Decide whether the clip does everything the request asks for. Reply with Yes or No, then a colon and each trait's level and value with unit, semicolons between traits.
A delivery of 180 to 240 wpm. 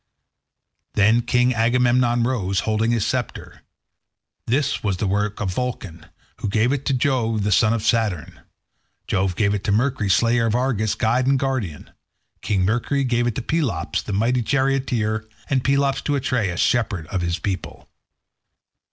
No: average, 160 wpm